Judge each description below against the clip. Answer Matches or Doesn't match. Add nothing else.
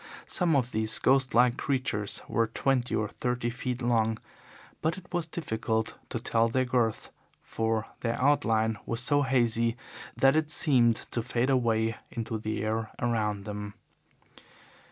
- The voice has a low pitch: Matches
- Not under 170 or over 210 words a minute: Doesn't match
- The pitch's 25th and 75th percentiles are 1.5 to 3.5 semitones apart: Matches